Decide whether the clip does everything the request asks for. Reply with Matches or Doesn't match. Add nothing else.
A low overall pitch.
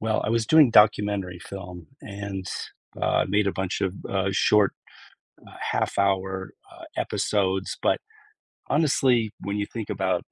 Matches